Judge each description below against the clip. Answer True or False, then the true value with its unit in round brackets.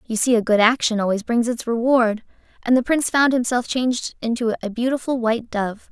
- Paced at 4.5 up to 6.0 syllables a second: True (5.7 syllables/s)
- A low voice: False (235 Hz)